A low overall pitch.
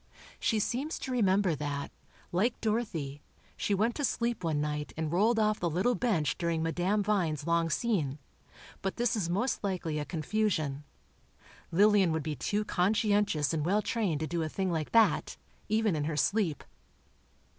No: medium, 185 Hz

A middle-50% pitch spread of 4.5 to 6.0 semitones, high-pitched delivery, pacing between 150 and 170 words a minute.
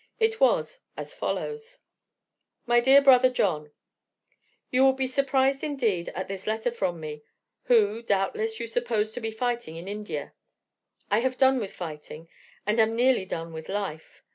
Yes: wide, 5.5 semitones; high, 225 Hz; average, 160 wpm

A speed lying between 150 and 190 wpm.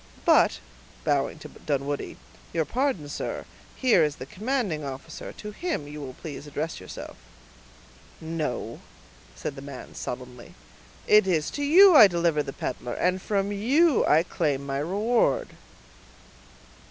No: average, 140 wpm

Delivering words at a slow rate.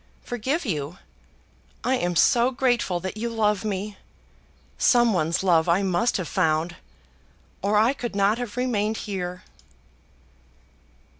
Yes: slow, 130 wpm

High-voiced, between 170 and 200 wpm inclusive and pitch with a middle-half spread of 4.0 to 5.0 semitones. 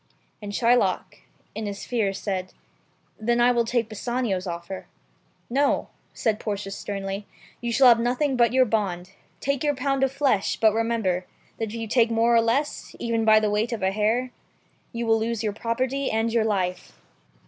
No: high, 225 Hz; average, 180 wpm; average, 2.8 semitones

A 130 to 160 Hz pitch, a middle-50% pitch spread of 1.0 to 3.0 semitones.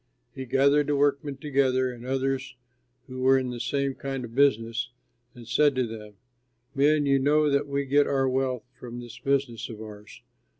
Yes: low, 135 Hz; narrow, 2.6 semitones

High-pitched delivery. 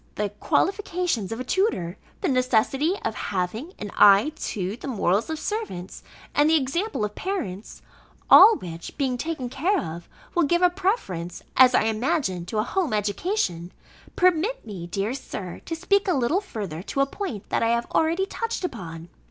Yes: very high, 255 Hz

